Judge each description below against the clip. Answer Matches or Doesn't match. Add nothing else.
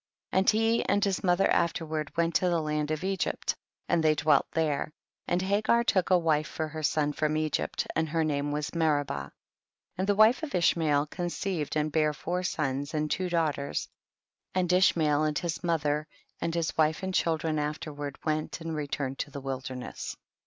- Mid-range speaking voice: Matches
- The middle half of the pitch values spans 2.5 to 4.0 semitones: Matches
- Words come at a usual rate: Doesn't match